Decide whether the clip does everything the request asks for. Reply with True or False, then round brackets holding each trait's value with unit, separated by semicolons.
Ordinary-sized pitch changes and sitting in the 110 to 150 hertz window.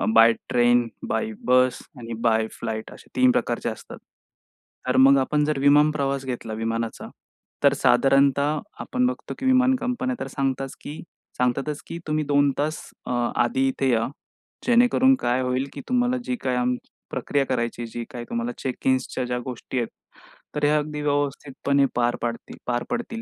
True (3.6 semitones; 135 Hz)